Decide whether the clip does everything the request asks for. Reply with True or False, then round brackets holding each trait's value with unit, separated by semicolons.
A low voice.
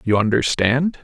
True (130 Hz)